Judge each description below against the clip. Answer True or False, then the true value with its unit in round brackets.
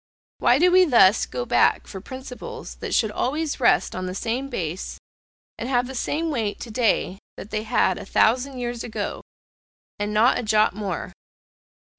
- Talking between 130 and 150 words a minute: False (175 wpm)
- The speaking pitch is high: True (235 Hz)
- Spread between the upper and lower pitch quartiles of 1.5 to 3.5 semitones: False (4.1 semitones)